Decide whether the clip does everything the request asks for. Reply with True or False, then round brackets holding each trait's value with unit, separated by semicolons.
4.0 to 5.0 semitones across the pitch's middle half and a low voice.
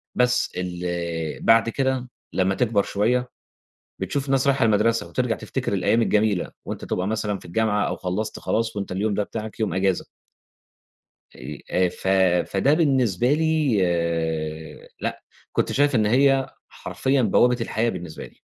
True (4.7 semitones; 110 Hz)